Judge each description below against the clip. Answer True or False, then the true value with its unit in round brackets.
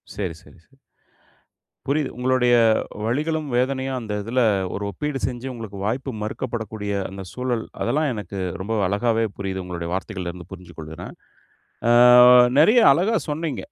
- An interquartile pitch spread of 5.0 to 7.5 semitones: True (5.3 semitones)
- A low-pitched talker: True (115 Hz)